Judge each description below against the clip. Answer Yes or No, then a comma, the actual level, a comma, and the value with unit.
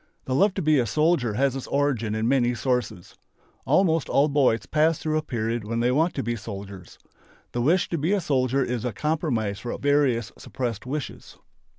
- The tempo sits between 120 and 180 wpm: No, average, 195 wpm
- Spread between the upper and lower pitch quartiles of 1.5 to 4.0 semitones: No, average, 4.6 semitones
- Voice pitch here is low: Yes, low, 130 Hz